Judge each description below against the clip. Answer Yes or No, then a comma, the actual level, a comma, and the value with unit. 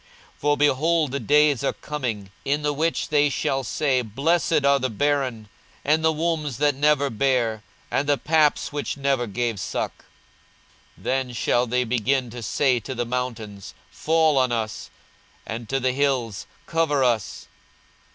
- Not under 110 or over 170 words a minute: Yes, average, 160 wpm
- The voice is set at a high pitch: No, low, 135 Hz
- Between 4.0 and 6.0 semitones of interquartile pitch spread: No, average, 3.5 semitones